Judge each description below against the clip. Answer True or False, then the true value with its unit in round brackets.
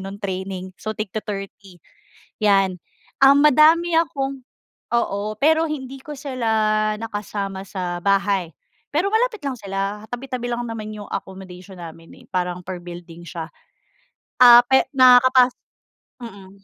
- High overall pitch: True (210 Hz)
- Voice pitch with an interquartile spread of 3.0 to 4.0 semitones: False (5.4 semitones)